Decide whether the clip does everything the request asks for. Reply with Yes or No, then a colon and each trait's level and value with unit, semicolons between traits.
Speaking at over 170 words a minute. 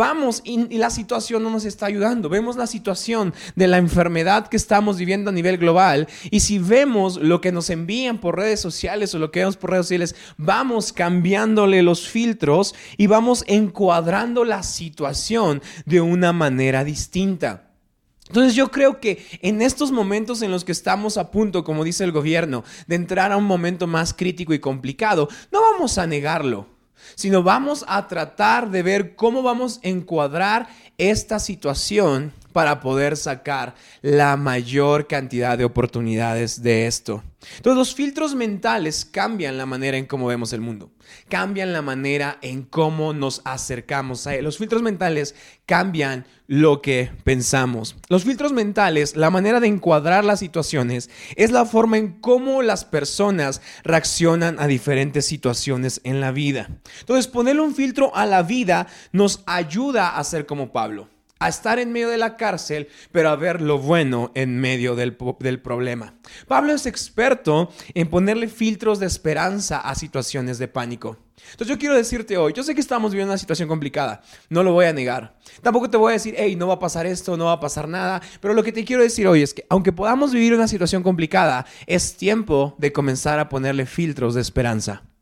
Yes: average, 180 wpm